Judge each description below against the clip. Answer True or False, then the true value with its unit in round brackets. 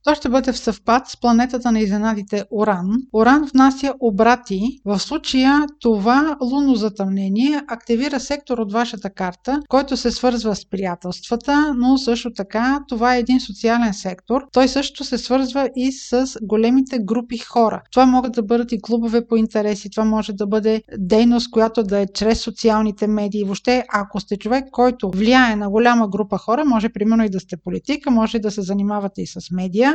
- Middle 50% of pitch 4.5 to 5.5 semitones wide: False (3.3 semitones)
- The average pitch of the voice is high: True (230 Hz)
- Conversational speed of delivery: False (175 wpm)